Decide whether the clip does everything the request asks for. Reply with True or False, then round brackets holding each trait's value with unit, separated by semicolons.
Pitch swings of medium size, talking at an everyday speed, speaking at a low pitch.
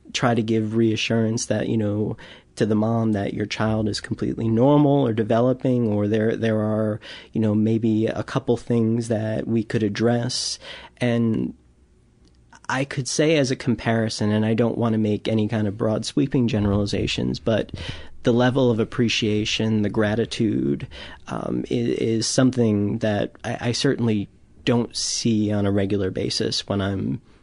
False (2.0 semitones; 160 wpm; 110 Hz)